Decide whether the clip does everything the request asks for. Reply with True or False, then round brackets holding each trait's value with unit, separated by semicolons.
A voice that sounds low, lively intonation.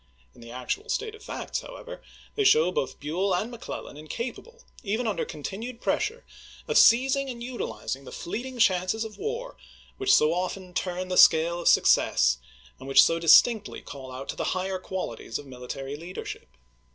False (185 Hz; 8.4 semitones)